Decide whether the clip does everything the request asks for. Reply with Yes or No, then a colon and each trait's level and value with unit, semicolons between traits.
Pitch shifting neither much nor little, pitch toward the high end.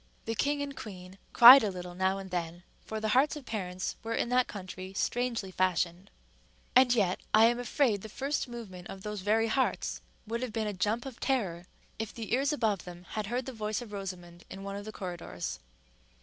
Yes: average, 4.4 semitones; high, 210 Hz